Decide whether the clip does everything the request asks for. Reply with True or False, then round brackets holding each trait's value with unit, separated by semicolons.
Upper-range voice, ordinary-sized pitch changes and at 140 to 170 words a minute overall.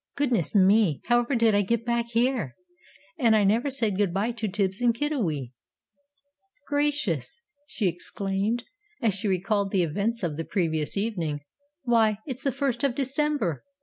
True (220 Hz; 4.2 semitones; 155 wpm)